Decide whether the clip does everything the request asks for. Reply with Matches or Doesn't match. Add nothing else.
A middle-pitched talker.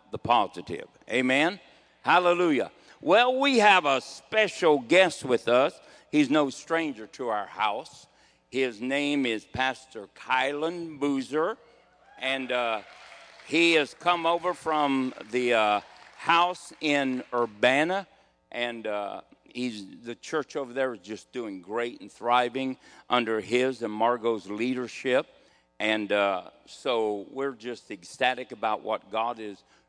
Doesn't match